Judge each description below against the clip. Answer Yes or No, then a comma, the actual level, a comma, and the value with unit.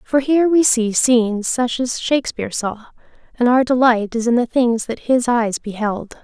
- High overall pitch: Yes, high, 240 Hz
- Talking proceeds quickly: No, average, 190 wpm